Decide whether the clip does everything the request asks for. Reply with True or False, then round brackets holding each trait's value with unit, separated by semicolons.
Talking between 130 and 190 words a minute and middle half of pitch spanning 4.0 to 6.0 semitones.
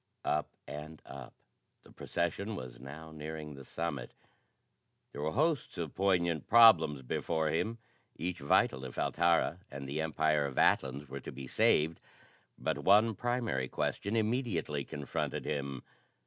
True (140 wpm; 4.7 semitones)